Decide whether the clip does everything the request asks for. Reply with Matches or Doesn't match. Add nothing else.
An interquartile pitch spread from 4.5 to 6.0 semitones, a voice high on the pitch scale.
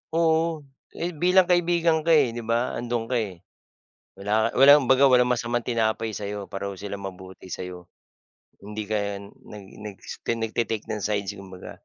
Doesn't match